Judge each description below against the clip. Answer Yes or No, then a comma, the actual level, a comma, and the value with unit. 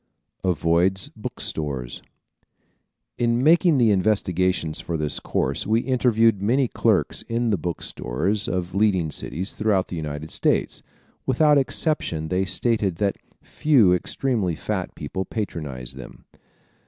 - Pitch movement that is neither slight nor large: No, wide, 5.8 semitones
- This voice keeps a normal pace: No, slow, 130 wpm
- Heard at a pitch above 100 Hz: No, very low, 95 Hz